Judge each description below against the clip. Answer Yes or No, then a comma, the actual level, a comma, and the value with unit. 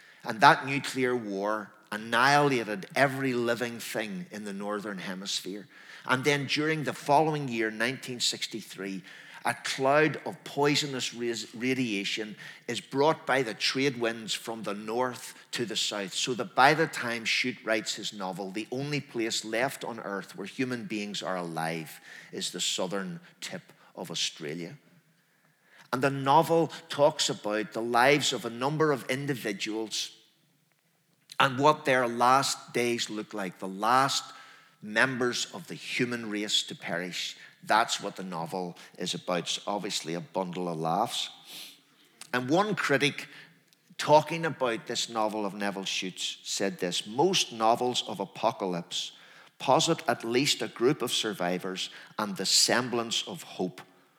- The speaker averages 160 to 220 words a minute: No, average, 145 wpm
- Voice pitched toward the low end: Yes, low, 120 Hz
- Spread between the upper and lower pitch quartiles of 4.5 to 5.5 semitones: Yes, average, 5.1 semitones